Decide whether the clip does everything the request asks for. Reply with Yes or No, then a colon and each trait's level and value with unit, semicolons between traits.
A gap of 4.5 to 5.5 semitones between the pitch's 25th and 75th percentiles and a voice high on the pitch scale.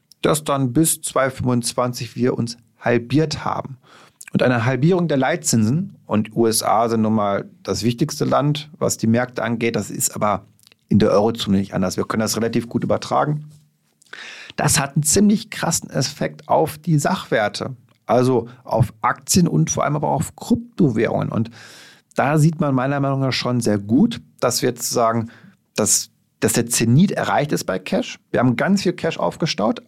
No: average, 5.0 semitones; low, 125 Hz